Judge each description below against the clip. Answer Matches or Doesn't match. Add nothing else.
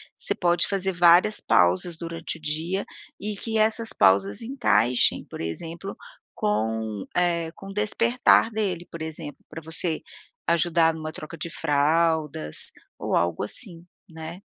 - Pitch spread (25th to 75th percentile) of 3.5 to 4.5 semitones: Matches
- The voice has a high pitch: Doesn't match